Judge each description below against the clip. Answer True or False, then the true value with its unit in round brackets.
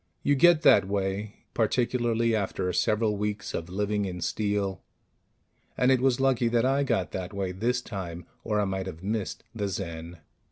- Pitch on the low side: True (105 Hz)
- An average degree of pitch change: True (3.5 semitones)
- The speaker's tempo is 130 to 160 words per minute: False (170 wpm)